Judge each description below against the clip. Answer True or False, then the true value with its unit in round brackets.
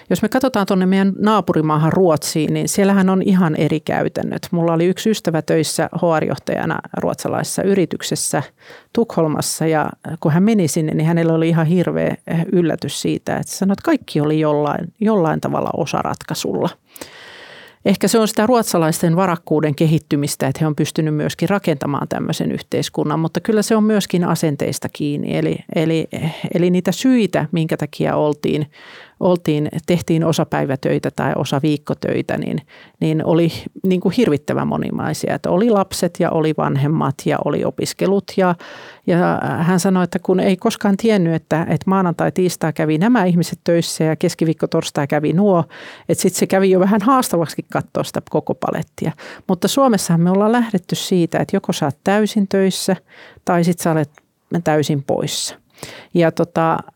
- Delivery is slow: False (155 wpm)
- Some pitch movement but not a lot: True (3.6 semitones)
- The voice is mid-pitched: True (175 Hz)